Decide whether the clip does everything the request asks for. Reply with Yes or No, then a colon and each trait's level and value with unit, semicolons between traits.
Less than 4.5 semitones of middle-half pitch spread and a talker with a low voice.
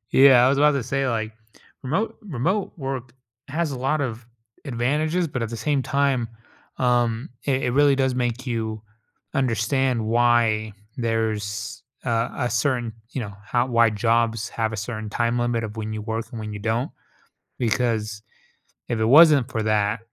Yes: average, 3.2 semitones; low, 120 Hz